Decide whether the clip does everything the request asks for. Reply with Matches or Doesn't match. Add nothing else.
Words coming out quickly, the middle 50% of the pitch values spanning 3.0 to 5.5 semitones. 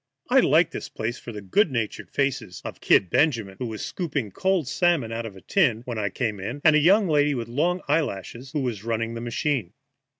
Matches